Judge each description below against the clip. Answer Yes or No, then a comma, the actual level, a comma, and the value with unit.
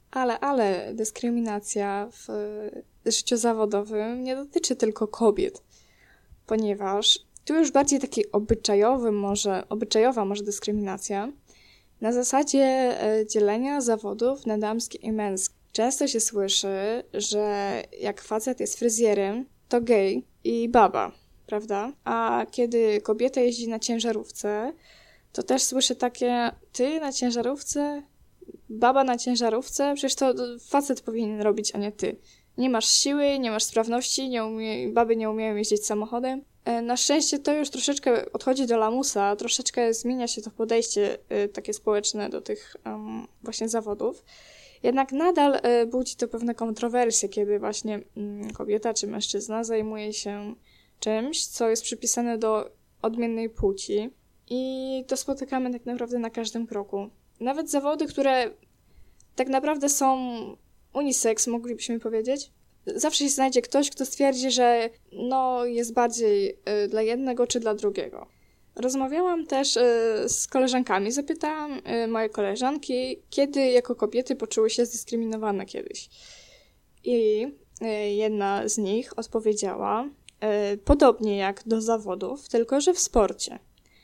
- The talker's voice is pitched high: Yes, high, 235 Hz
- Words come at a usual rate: Yes, average, 125 wpm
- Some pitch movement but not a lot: Yes, average, 3.5 semitones